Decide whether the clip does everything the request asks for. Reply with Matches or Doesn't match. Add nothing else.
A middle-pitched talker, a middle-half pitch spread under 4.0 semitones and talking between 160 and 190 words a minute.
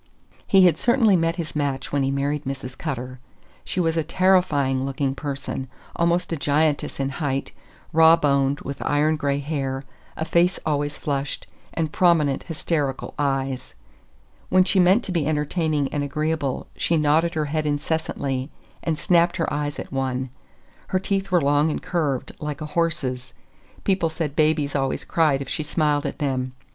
Matches